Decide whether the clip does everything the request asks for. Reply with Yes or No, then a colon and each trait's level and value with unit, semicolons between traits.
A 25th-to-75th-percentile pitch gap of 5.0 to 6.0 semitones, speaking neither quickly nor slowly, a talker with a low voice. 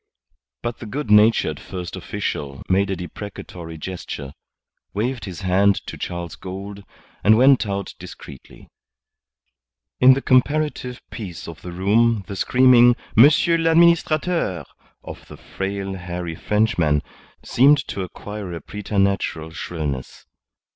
No: wide, 5.4 semitones; slow, 120 wpm; low, 100 Hz